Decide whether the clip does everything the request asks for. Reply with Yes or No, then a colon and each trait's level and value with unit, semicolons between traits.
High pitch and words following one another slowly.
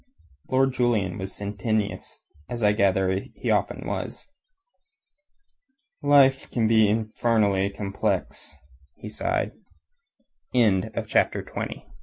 No: low, 105 Hz; slow, 95 wpm